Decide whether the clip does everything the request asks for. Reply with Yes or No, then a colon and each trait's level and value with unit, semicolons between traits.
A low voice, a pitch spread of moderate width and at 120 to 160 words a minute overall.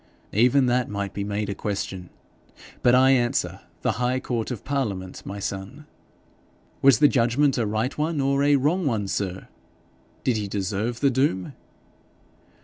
Yes: low, 120 Hz; average, 4.9 semitones; average, 150 wpm